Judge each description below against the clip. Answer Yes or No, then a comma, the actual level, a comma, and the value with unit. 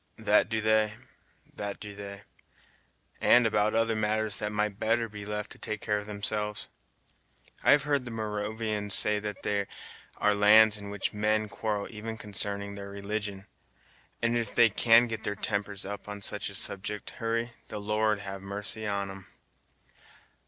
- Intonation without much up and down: Yes, narrow, 1.3 semitones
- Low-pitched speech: Yes, low, 105 Hz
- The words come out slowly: No, average, 165 wpm